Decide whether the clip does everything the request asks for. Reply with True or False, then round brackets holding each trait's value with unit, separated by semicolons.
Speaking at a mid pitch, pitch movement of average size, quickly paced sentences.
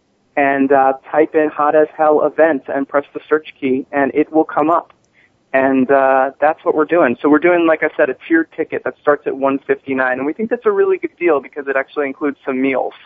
False (145 Hz; 2.3 semitones; 235 wpm)